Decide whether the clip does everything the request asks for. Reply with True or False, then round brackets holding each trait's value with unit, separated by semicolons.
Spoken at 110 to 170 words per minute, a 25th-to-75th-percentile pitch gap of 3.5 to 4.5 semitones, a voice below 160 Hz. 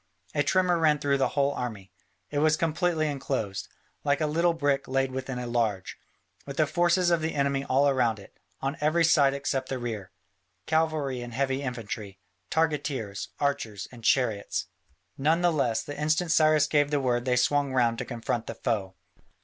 False (180 wpm; 4.2 semitones; 140 Hz)